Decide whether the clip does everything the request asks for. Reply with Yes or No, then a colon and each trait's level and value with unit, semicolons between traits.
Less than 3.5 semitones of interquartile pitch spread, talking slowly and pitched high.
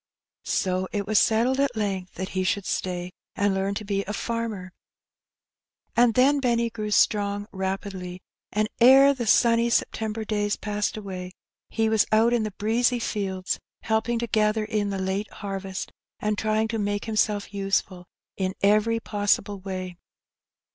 No: narrow, 2.5 semitones; average, 155 wpm; high, 210 Hz